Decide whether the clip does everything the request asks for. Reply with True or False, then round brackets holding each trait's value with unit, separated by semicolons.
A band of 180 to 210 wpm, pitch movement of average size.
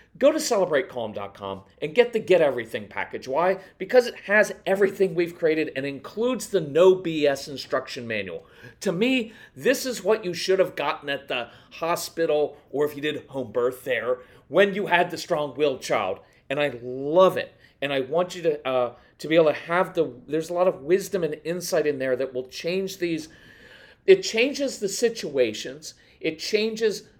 False (185 wpm; 6.0 semitones)